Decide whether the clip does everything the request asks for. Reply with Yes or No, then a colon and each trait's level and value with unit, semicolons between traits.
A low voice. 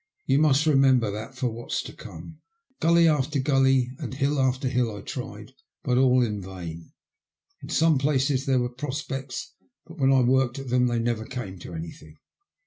Yes: low, 130 Hz